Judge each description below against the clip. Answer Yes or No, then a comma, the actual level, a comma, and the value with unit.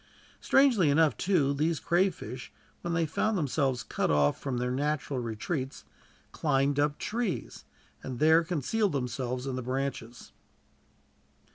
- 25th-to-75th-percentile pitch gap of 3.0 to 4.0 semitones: No, average, 4.6 semitones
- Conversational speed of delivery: No, slow, 130 wpm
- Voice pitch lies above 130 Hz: Yes, medium, 140 Hz